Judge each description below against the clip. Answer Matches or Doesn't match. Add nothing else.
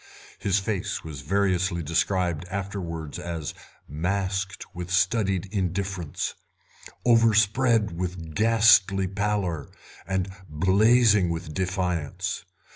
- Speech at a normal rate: Doesn't match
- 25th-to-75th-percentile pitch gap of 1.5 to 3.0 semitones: Matches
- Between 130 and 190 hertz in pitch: Doesn't match